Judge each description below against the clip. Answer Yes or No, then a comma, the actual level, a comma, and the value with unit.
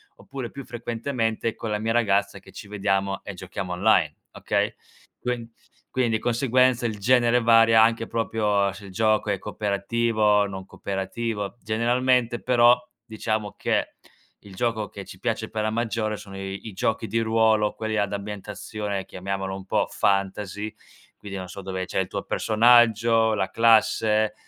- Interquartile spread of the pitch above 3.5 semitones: No, narrow, 2.6 semitones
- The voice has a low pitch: Yes, low, 110 Hz